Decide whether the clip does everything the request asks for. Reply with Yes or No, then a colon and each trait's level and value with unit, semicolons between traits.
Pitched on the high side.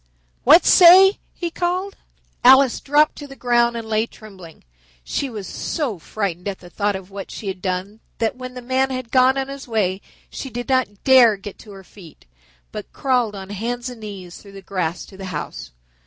Yes: high, 225 Hz